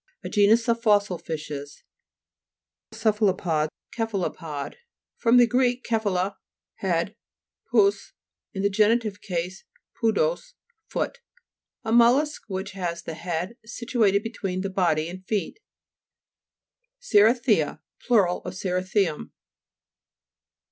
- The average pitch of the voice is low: No, high, 200 Hz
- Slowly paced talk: Yes, slow, 105 wpm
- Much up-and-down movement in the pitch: No, average, 4.2 semitones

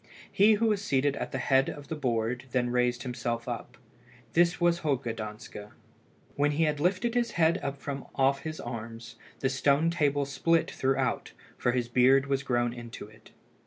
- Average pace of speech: Yes, average, 180 wpm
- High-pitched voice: No, low, 135 Hz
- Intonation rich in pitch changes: No, average, 4.3 semitones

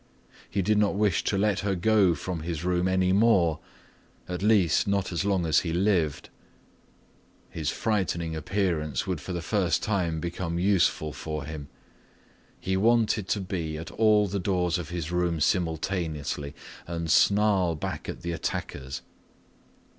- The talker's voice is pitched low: Yes, very low, 90 Hz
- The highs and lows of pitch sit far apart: No, average, 3.3 semitones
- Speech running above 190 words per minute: No, average, 155 wpm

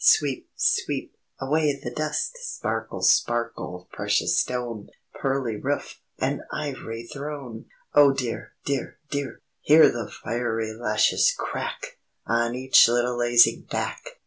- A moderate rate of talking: No, slow, 120 wpm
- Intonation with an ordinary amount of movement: Yes, average, 3.3 semitones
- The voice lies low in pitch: Yes, low, 125 Hz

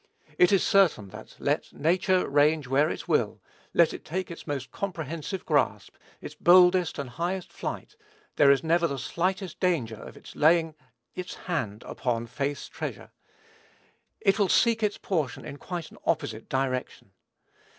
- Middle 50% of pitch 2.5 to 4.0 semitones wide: No, average, 4.8 semitones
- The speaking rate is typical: Yes, average, 155 wpm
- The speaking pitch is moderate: Yes, medium, 160 Hz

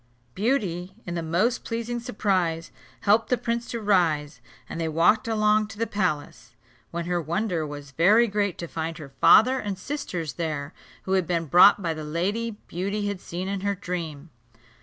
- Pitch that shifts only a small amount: No, average, 4.3 semitones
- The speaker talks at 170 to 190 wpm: Yes, average, 180 wpm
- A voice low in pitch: No, medium, 185 Hz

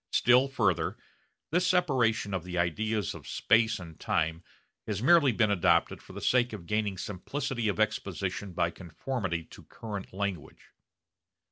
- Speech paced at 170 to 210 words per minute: No, average, 145 wpm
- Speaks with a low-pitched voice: Yes, low, 105 Hz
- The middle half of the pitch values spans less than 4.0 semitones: No, average, 4.9 semitones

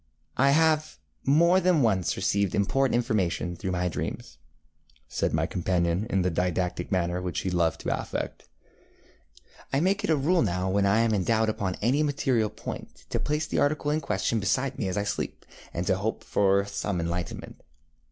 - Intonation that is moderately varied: No, wide, 7.2 semitones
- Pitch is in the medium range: No, low, 100 Hz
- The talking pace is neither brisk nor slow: Yes, average, 180 wpm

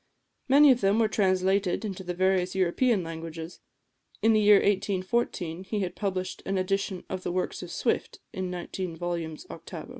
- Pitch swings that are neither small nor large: No, narrow, 2.3 semitones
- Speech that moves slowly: No, average, 170 wpm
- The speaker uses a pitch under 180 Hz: No, medium, 185 Hz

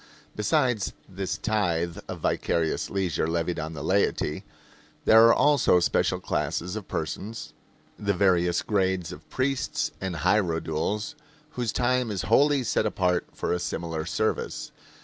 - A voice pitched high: No, very low, 95 Hz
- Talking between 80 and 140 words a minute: Yes, slow, 135 wpm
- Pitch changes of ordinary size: Yes, average, 4.5 semitones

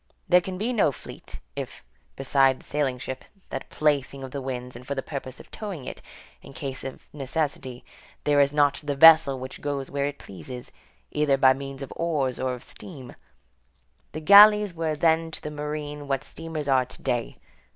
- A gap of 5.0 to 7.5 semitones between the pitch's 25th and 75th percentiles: No, average, 2.7 semitones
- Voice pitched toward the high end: No, medium, 140 Hz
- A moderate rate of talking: Yes, average, 190 wpm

